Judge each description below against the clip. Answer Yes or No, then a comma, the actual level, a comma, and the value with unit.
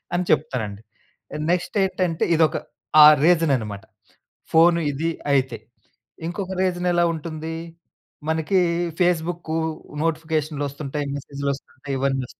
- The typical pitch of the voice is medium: Yes, medium, 160 Hz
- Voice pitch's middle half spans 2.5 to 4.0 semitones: Yes, average, 3.7 semitones